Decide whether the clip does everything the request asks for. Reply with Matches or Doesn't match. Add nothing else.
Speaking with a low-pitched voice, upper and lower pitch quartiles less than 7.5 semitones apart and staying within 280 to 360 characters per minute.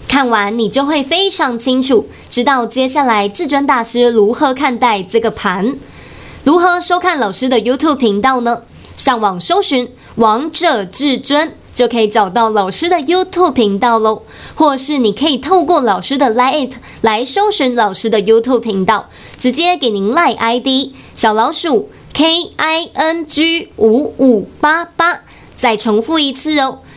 Doesn't match